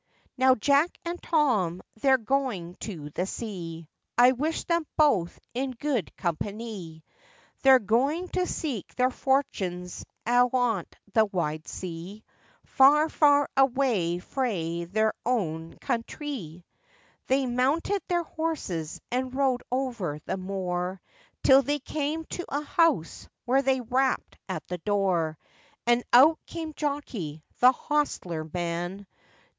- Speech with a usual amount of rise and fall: No, wide, 7.6 semitones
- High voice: Yes, high, 245 Hz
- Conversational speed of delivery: No, slow, 125 wpm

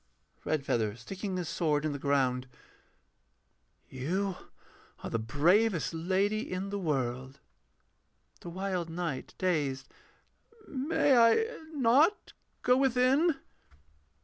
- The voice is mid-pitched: Yes, medium, 180 Hz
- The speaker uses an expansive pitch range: Yes, wide, 8.2 semitones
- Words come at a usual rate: No, slow, 100 wpm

